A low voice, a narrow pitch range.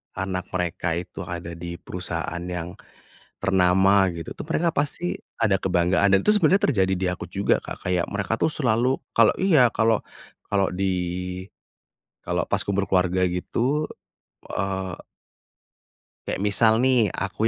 No: very low, 95 Hz; average, 4.1 semitones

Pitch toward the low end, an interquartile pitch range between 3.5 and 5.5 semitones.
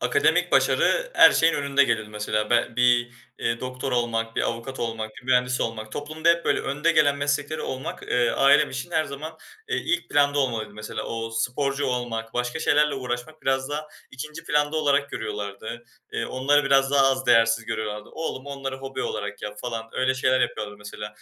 Yes: low, 130 Hz; average, 3.9 semitones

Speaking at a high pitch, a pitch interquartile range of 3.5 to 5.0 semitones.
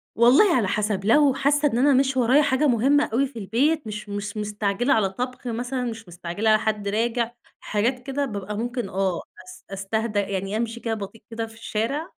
Yes: high, 225 Hz; average, 4.0 semitones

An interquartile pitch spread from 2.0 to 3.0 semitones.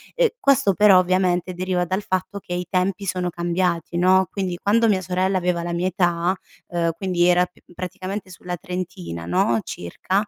No: narrow, 1.4 semitones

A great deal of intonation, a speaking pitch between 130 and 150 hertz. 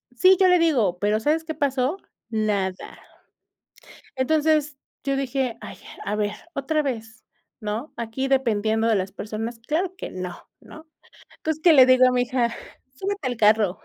No: wide, 5.7 semitones; very high, 255 Hz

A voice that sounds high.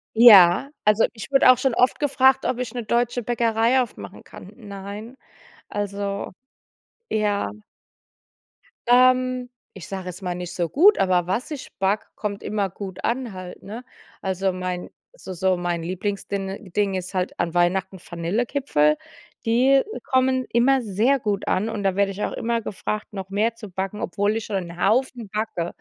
Yes: high, 205 Hz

